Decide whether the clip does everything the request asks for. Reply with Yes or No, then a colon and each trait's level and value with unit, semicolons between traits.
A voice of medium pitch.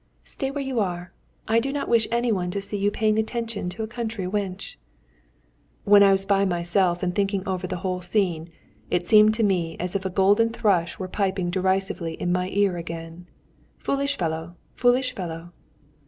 No: high, 195 Hz